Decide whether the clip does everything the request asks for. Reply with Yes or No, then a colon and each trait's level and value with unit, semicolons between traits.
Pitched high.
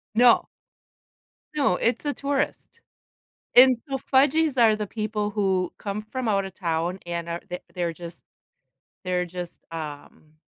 Yes: high, 200 Hz